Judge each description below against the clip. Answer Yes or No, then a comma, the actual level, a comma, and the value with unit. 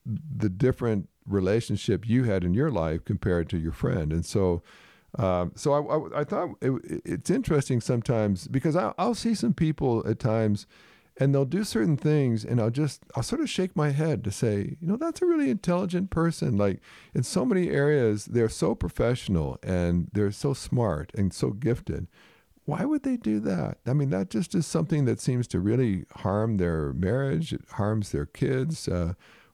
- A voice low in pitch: Yes, low, 125 Hz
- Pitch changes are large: Yes, wide, 7.5 semitones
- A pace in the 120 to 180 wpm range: No, average, 195 wpm